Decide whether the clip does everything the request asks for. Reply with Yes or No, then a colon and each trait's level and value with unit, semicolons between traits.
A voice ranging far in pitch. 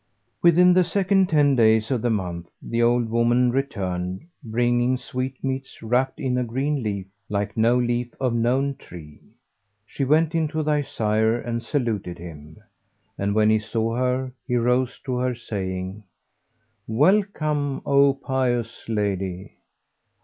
No: average, 3.8 semitones